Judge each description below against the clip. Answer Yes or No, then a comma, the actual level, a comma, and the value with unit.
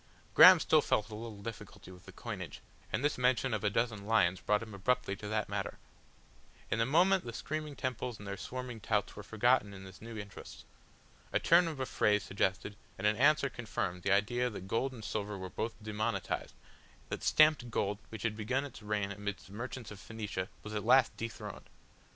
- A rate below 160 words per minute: No, average, 200 wpm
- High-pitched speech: No, low, 110 Hz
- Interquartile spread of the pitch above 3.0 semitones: Yes, average, 3.5 semitones